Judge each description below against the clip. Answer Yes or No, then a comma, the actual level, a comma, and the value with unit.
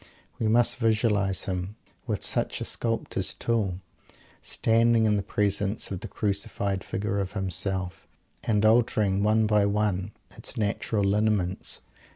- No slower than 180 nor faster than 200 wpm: No, slow, 135 wpm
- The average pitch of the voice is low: Yes, low, 105 Hz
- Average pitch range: No, narrow, 2.1 semitones